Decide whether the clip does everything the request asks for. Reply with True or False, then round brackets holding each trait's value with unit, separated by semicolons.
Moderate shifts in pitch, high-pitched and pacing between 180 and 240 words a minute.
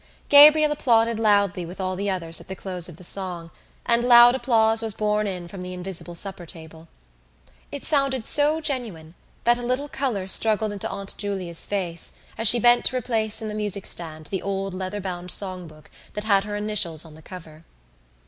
True (4.1 semitones; 200 Hz; 190 wpm)